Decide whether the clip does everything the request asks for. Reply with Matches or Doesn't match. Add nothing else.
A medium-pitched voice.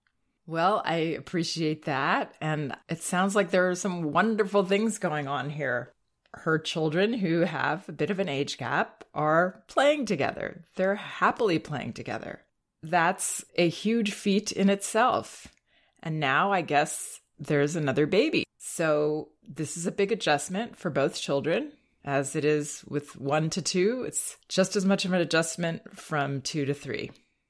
Matches